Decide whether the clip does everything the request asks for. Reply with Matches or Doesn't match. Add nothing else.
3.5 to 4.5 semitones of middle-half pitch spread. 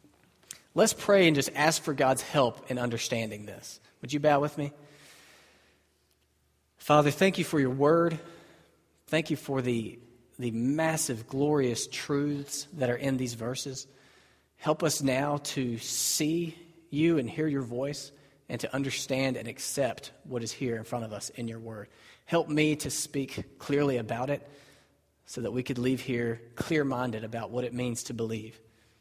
Matches